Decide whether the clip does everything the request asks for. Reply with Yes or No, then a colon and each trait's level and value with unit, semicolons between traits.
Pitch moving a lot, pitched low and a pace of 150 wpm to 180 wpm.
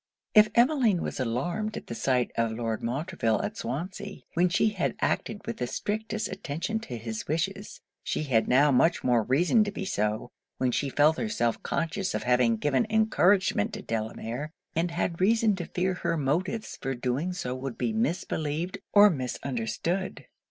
No: wide, 8.2 semitones; medium, 165 Hz; average, 170 wpm